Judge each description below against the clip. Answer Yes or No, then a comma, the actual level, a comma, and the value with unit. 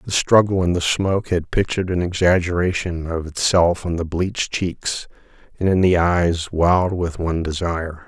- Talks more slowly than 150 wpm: No, average, 170 wpm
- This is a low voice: Yes, very low, 90 Hz